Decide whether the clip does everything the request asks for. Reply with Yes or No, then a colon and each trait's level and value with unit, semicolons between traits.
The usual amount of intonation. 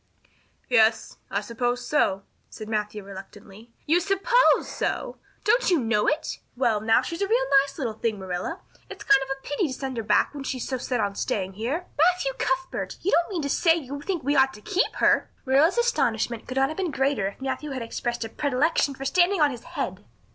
No: wide, 6.9 semitones